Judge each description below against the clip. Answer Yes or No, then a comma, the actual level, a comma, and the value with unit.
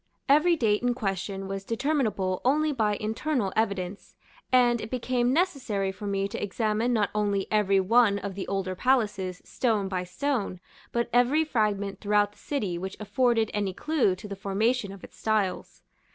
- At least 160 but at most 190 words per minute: Yes, average, 165 wpm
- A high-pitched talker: Yes, high, 210 Hz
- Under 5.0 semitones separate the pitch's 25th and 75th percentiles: Yes, average, 4.0 semitones